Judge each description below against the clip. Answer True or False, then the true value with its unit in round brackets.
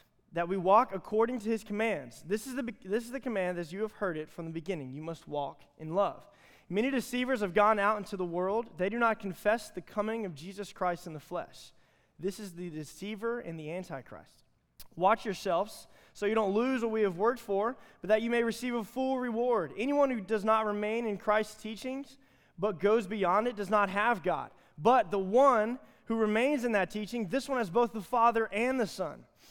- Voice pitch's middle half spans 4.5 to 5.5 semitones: False (4.0 semitones)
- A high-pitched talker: True (210 Hz)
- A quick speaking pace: True (220 wpm)